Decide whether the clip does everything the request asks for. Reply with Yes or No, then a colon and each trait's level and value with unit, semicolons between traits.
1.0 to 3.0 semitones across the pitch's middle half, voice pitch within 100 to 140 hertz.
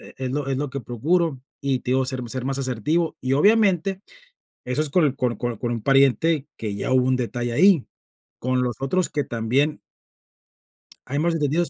No: average, 3.7 semitones; low, 135 Hz